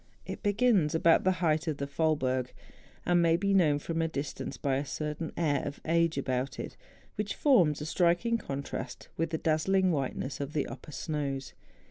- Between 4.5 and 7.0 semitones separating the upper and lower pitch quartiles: No, average, 3.5 semitones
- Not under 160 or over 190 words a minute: Yes, average, 180 wpm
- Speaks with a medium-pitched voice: Yes, medium, 155 Hz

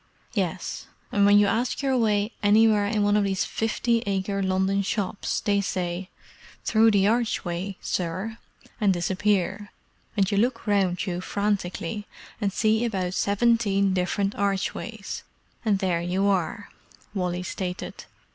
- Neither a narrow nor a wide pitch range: No, narrow, 2.1 semitones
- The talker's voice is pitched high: Yes, high, 200 Hz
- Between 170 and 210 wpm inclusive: No, slow, 135 wpm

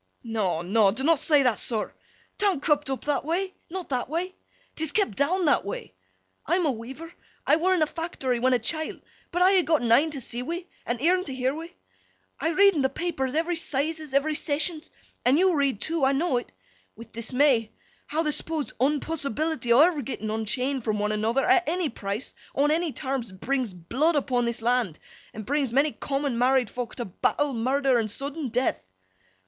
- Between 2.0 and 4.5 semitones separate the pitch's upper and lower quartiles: No, average, 4.9 semitones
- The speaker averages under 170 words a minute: No, average, 185 wpm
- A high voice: Yes, very high, 275 Hz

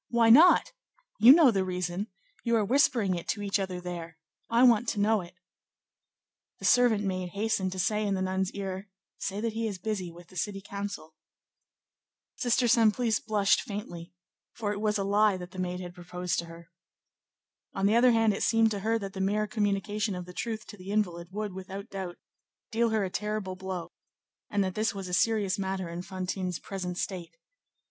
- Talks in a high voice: Yes, high, 200 Hz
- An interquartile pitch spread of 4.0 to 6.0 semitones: No, average, 2.8 semitones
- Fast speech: No, average, 195 wpm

